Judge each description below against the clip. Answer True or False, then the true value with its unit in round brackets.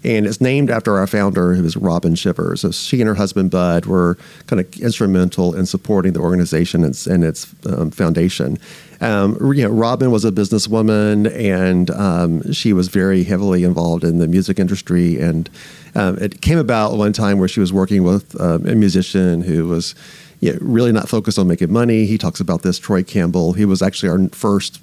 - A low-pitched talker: True (95 Hz)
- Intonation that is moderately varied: True (3.4 semitones)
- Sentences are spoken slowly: False (205 wpm)